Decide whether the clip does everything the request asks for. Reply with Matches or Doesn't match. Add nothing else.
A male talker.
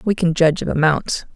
Doesn't match